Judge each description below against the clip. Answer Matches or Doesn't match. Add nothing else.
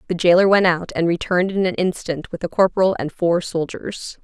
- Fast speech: Matches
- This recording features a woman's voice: Matches